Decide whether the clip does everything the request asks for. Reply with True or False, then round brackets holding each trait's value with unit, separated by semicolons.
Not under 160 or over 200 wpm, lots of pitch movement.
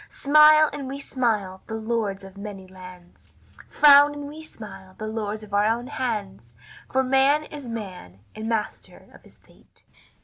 True (165 wpm; 6.0 semitones)